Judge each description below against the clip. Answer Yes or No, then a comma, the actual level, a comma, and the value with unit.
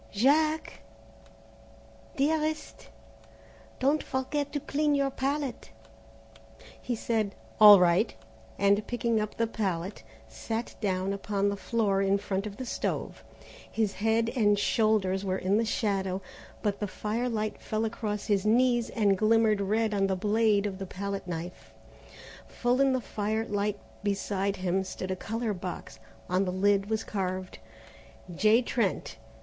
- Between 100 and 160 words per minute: Yes, average, 140 wpm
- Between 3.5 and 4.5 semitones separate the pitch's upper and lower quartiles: No, average, 2.9 semitones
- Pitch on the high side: Yes, high, 210 Hz